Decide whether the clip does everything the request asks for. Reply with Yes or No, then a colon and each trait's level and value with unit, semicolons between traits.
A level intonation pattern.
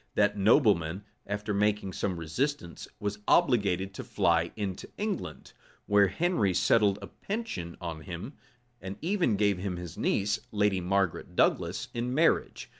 No: average, 3.5 semitones